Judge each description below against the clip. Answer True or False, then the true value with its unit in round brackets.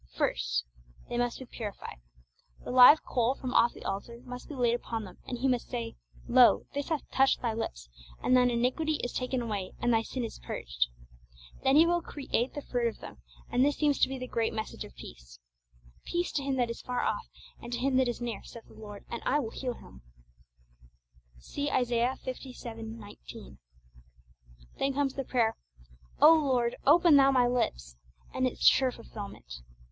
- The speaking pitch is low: False (245 Hz)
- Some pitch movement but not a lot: True (3.0 semitones)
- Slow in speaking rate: False (190 wpm)